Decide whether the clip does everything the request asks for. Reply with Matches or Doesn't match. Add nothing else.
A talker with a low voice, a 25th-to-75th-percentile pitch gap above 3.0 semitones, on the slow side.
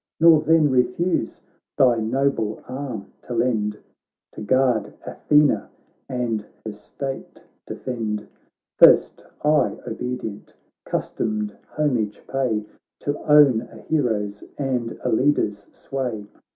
Matches